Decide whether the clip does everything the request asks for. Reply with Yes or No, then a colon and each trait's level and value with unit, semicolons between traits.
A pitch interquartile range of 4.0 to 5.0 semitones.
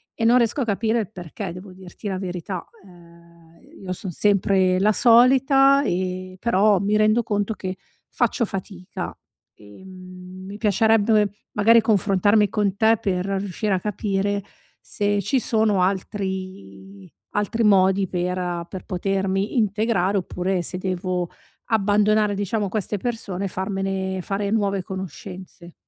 No: narrow, 2.4 semitones